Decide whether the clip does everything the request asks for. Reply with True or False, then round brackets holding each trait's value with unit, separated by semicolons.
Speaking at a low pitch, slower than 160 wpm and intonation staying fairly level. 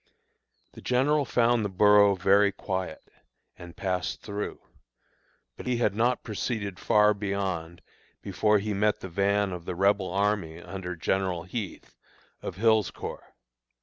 True (100 Hz; 140 wpm; 2.3 semitones)